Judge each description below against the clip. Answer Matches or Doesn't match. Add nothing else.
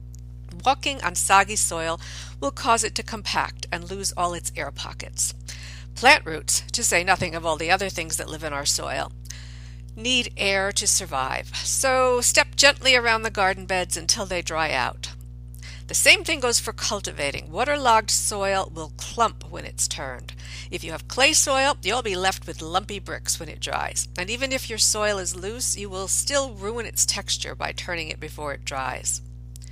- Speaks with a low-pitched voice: Matches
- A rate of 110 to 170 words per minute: Doesn't match